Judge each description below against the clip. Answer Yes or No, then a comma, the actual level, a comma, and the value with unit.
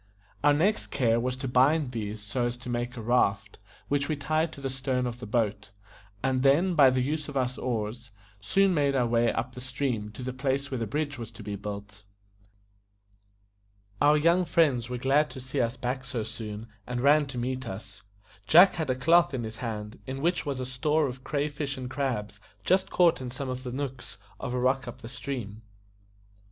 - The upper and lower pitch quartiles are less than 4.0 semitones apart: Yes, average, 3.2 semitones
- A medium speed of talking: No, fast, 210 wpm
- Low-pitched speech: Yes, low, 130 Hz